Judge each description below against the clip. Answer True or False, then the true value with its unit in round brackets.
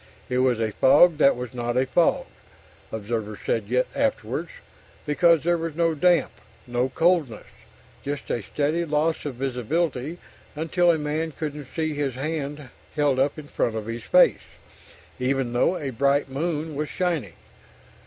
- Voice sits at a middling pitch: True (145 Hz)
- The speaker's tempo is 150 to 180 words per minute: True (155 wpm)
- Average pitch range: True (4.2 semitones)